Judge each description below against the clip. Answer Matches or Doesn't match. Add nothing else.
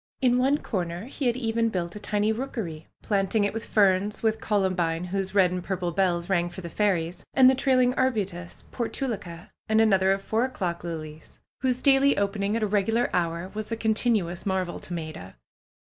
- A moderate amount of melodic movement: Matches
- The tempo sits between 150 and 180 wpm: Doesn't match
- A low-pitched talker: Doesn't match